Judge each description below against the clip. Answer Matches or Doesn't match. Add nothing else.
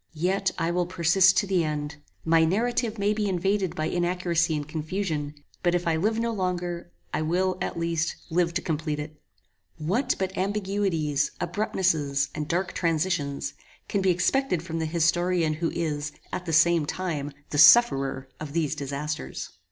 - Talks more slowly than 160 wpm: Doesn't match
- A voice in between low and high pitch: Matches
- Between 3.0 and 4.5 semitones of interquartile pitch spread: Matches